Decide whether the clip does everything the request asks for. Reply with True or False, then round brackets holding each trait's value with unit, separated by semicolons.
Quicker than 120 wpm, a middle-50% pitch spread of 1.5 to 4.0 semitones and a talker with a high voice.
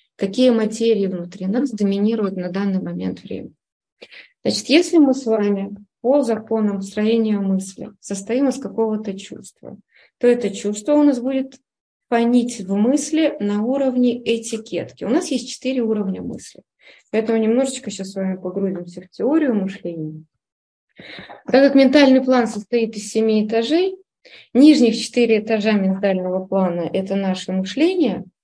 False (135 wpm; 4.6 semitones; 220 Hz)